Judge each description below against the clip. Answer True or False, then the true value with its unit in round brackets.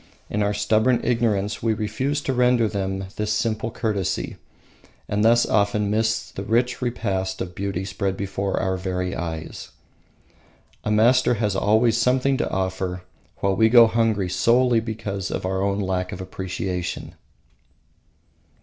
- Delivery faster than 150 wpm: False (145 wpm)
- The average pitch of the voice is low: True (105 Hz)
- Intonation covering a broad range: False (3.2 semitones)